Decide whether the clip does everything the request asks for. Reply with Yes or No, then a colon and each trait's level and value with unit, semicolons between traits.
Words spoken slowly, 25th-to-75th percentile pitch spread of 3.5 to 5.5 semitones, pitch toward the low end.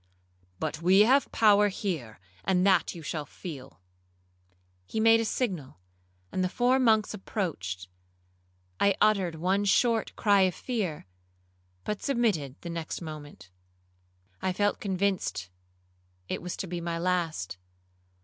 No: slow, 130 wpm; average, 4.6 semitones; medium, 185 Hz